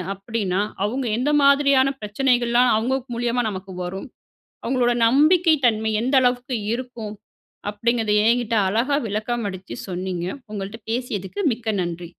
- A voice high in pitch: Yes, high, 235 Hz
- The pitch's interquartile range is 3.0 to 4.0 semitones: Yes, average, 3.7 semitones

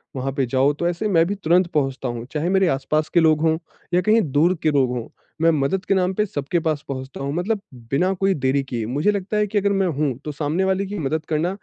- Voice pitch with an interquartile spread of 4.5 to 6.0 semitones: Yes, average, 5.3 semitones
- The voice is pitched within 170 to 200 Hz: No, medium, 160 Hz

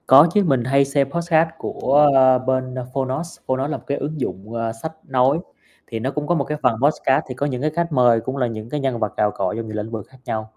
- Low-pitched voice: Yes, low, 130 Hz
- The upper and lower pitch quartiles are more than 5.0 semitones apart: No, average, 3.9 semitones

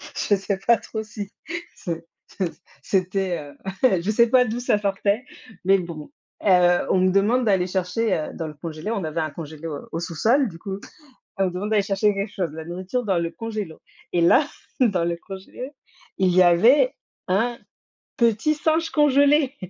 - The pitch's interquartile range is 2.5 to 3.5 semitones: No, average, 4.6 semitones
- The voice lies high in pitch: Yes, high, 195 Hz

